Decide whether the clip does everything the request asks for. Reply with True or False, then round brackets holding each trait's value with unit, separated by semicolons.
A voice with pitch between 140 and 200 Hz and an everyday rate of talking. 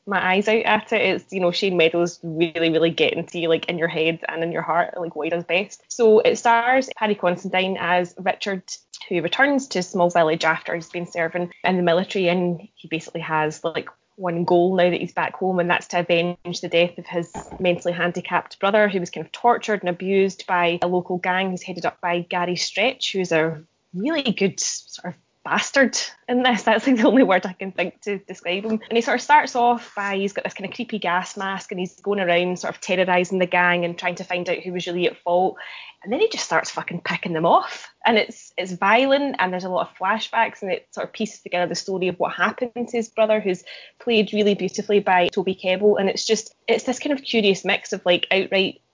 False (185 Hz; 235 wpm)